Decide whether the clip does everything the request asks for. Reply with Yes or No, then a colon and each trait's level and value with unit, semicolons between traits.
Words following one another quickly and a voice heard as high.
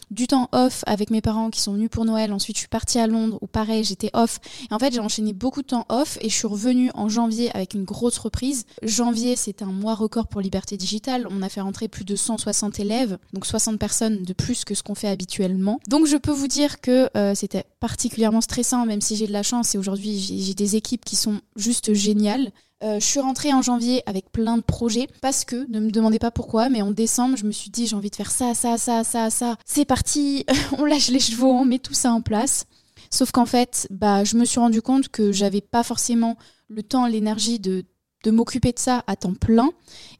Yes: fast, 240 wpm; high, 225 Hz